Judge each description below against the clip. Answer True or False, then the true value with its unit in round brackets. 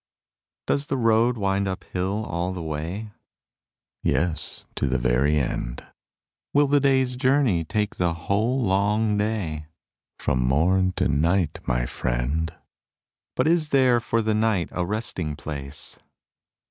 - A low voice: True (95 Hz)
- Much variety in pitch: True (6.5 semitones)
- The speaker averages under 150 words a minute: True (135 wpm)